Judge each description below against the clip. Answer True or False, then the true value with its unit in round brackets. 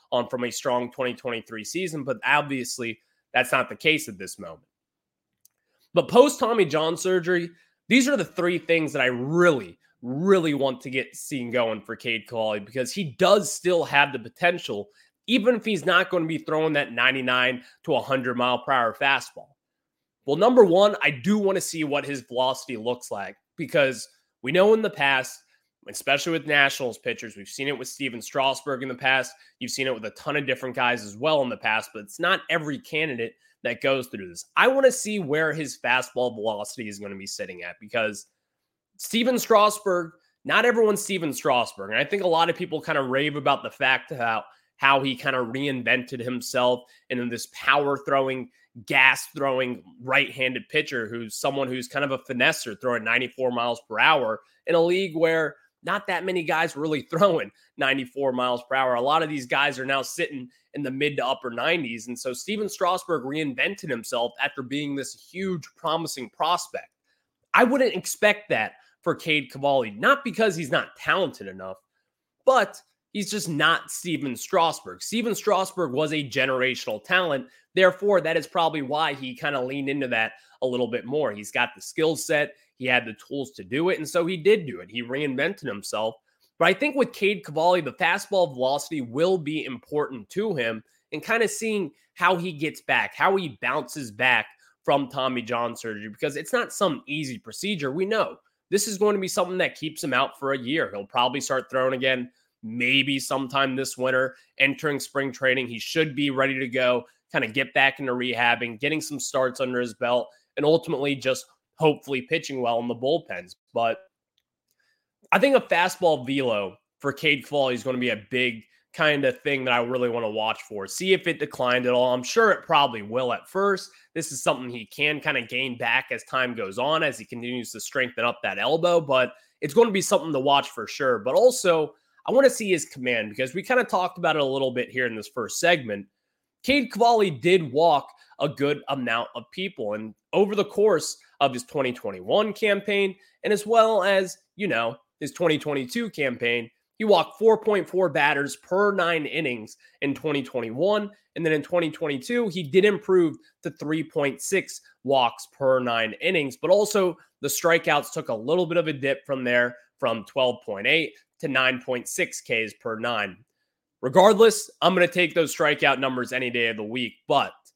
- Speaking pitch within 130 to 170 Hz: True (140 Hz)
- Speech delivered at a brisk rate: False (195 wpm)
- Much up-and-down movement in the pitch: True (5.9 semitones)